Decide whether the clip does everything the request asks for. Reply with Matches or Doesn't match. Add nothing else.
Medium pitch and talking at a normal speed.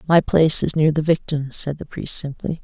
Doesn't match